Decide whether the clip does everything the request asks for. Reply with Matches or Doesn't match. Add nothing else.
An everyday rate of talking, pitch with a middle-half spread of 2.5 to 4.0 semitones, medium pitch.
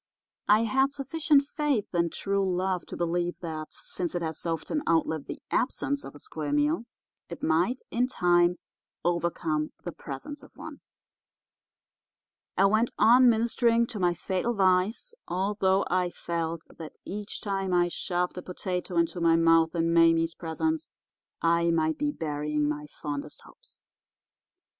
Doesn't match